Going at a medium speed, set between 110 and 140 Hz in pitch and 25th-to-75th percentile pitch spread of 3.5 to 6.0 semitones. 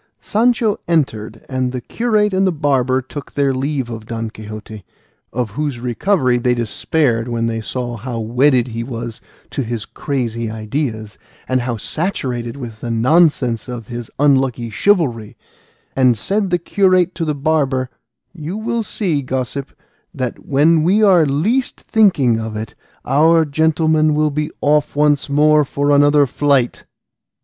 Yes: average, 150 wpm; low, 135 Hz; average, 4.8 semitones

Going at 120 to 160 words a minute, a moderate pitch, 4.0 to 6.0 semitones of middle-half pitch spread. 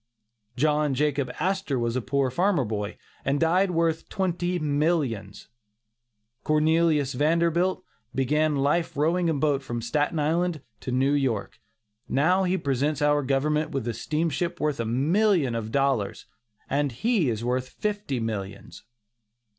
Yes: average, 140 wpm; medium, 145 Hz; average, 4.5 semitones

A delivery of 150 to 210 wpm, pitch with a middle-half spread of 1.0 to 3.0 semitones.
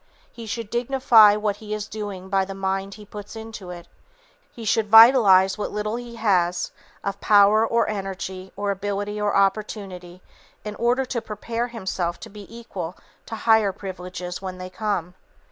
Yes: average, 165 wpm; narrow, 2.6 semitones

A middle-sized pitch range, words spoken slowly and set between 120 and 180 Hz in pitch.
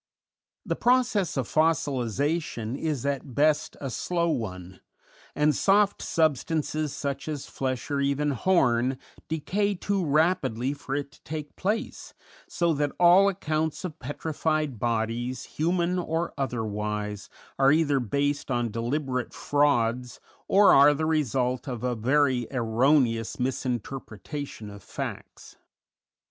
Yes: average, 4.5 semitones; slow, 125 wpm; medium, 140 Hz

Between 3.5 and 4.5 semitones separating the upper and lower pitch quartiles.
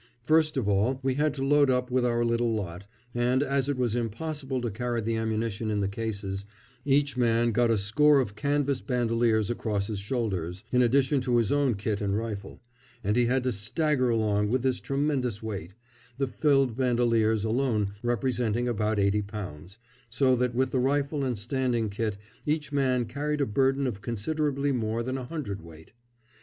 Yes: average, 3.8 semitones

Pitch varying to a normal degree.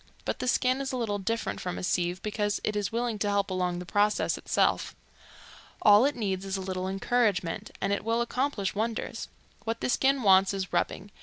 Yes: average, 3.4 semitones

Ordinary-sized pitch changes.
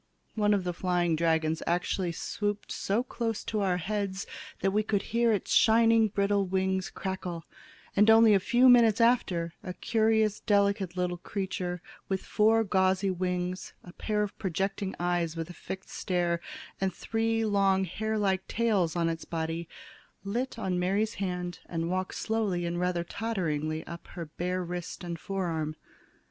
Yes: average, 3.1 semitones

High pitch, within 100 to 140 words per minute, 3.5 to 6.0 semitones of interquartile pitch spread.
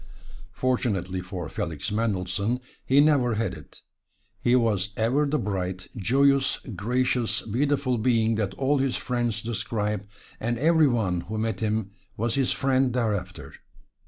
No: low, 115 Hz; slow, 135 wpm; average, 4.0 semitones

